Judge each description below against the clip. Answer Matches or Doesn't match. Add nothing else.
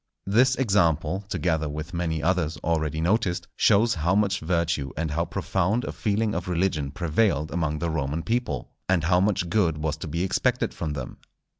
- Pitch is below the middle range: Matches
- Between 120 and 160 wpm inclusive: Doesn't match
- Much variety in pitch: Doesn't match